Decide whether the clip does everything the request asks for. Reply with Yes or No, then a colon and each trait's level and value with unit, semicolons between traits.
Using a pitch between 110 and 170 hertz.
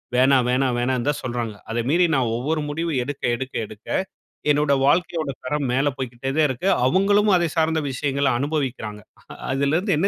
Yes: medium, 140 Hz